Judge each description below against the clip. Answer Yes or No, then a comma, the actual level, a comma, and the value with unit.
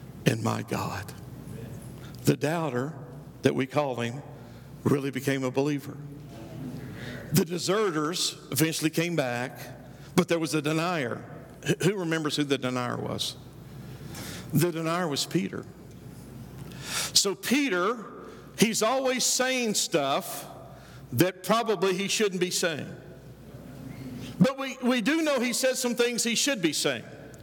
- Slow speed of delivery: Yes, slow, 125 wpm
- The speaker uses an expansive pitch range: Yes, wide, 5.9 semitones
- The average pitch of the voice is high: No, medium, 160 Hz